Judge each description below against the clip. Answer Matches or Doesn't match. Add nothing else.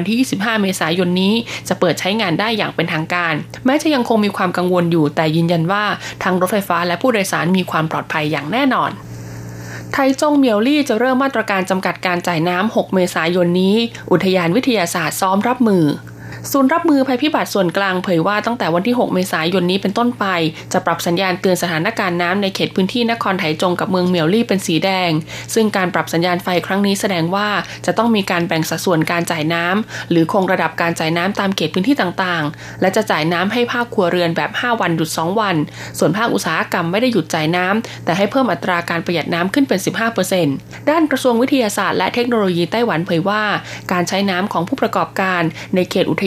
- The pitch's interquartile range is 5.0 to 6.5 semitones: Doesn't match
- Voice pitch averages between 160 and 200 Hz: Matches